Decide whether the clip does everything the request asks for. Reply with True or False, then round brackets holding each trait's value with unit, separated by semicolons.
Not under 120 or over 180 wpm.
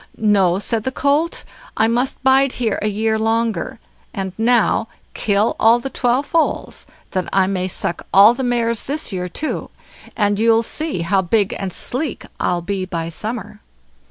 True (165 wpm)